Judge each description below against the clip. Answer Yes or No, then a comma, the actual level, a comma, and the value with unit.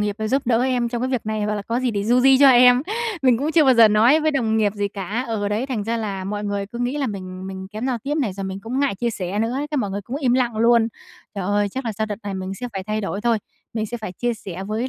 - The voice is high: Yes, high, 225 Hz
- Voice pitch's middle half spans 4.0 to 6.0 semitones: No, average, 3.5 semitones